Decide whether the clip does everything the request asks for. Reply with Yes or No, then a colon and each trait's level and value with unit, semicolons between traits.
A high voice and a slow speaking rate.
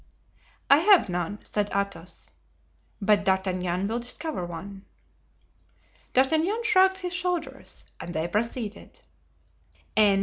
Yes: high, 210 Hz; slow, 100 wpm